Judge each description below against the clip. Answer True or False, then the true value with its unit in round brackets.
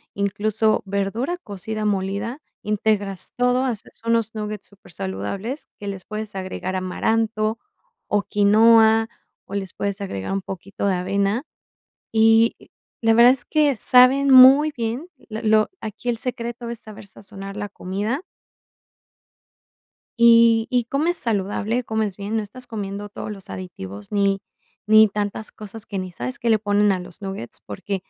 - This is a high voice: True (215 Hz)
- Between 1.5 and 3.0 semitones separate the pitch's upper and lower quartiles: True (2.7 semitones)